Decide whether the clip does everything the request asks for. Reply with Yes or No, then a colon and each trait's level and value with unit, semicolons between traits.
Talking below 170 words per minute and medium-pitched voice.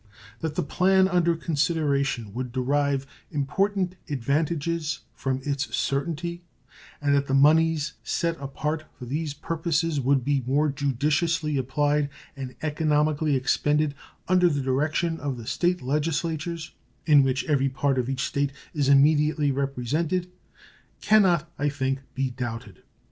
Yes: slow, 135 wpm; medium, 145 Hz